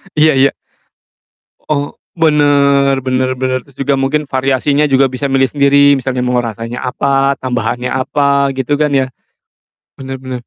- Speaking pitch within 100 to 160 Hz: Yes, low, 135 Hz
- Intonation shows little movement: Yes, narrow, 1.6 semitones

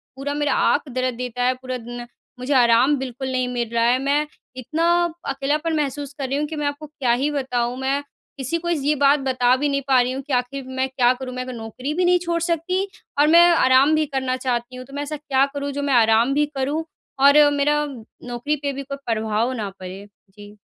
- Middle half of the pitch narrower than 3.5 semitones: Yes, average, 2.8 semitones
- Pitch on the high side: Yes, very high, 270 Hz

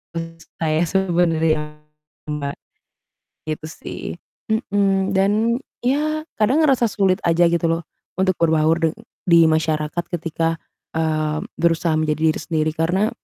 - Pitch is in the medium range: Yes, medium, 165 Hz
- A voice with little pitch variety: No, average, 3.6 semitones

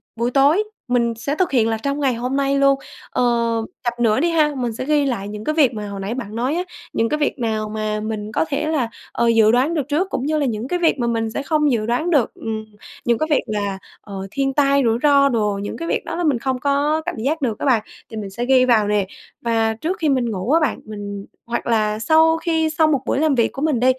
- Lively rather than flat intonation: No, average, 4.8 semitones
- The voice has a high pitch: Yes, very high, 250 Hz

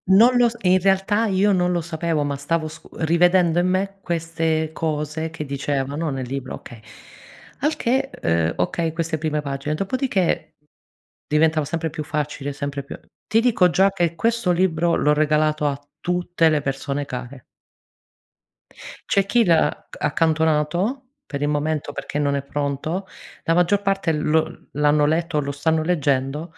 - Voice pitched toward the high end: No, medium, 160 Hz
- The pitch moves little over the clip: No, average, 3.4 semitones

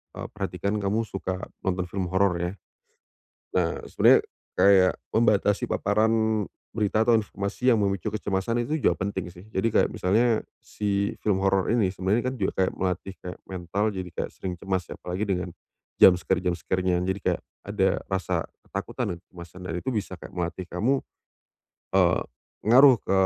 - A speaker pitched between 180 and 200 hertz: No, very low, 95 Hz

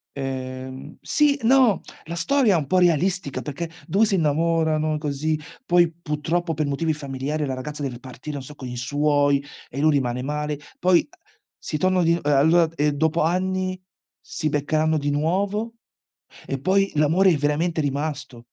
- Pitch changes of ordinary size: Yes, average, 3.5 semitones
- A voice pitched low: No, medium, 155 Hz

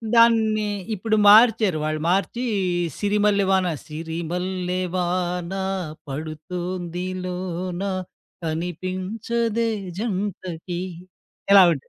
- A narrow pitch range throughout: No, average, 3.0 semitones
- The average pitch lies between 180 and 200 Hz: Yes, medium, 185 Hz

